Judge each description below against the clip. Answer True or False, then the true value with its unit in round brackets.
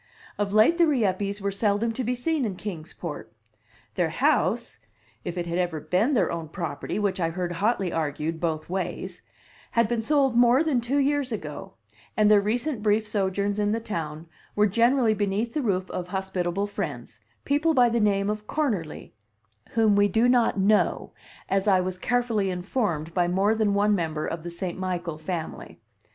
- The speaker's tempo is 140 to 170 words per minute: False (180 wpm)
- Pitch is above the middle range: True (200 Hz)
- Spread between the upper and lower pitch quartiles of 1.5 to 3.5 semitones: False (4.5 semitones)